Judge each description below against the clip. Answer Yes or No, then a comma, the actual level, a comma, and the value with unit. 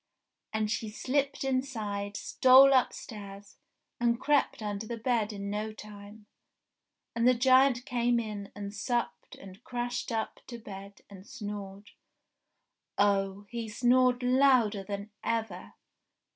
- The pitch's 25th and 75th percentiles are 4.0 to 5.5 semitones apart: No, average, 3.4 semitones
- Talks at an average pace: No, slow, 125 wpm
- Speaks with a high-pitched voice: Yes, high, 220 Hz